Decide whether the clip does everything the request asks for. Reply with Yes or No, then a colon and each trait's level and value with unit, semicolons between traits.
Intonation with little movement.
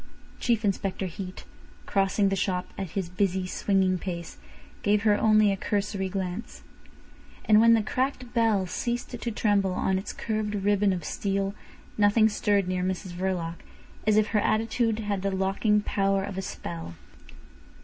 Yes: narrow, 2.2 semitones